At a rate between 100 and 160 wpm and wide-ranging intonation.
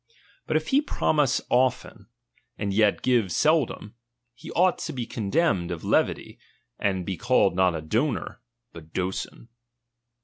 Yes: average, 140 wpm; wide, 5.7 semitones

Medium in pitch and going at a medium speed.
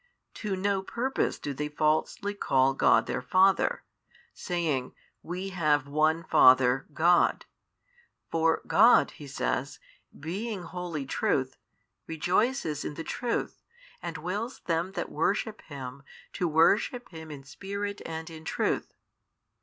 No: medium, 165 Hz; slow, 125 wpm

